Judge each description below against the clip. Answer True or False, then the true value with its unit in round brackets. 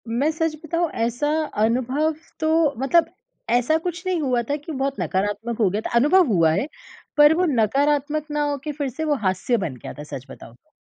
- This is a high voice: True (275 Hz)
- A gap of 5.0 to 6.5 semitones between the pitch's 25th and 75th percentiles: True (5.5 semitones)